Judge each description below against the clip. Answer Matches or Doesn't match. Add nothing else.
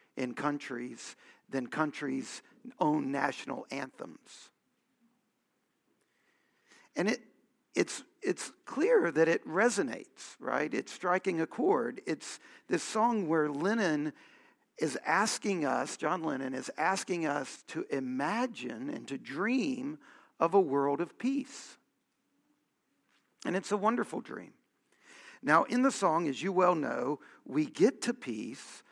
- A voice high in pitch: Matches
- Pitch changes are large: Matches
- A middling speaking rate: Doesn't match